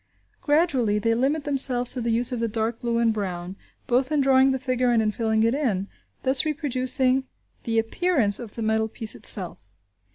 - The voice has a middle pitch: No, high, 240 Hz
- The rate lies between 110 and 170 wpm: No, average, 190 wpm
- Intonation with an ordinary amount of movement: Yes, average, 3.2 semitones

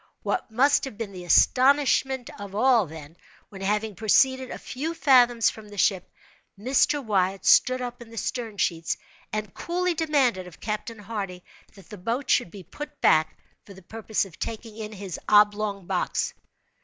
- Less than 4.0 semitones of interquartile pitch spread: No, average, 4.6 semitones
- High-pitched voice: Yes, high, 215 Hz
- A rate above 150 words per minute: Yes, average, 170 wpm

